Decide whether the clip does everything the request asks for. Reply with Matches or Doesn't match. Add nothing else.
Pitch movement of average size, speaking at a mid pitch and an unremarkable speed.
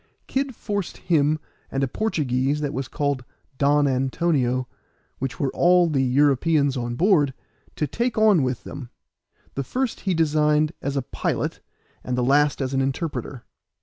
Matches